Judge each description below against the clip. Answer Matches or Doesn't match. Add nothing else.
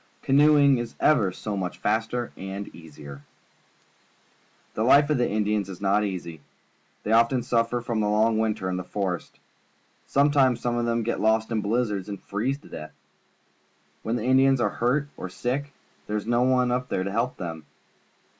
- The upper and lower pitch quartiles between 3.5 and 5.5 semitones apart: Matches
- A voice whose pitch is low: Matches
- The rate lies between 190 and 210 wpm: Doesn't match